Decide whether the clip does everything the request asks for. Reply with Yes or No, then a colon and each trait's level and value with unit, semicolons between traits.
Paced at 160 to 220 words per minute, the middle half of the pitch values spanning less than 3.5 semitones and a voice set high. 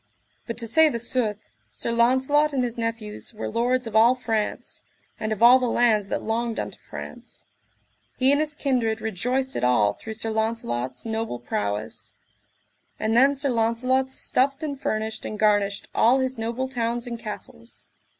Yes: average, 170 wpm; average, 2.8 semitones; high, 230 Hz